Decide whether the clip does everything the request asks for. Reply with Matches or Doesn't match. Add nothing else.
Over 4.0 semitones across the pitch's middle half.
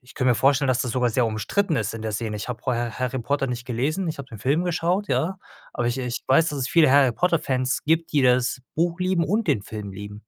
Matches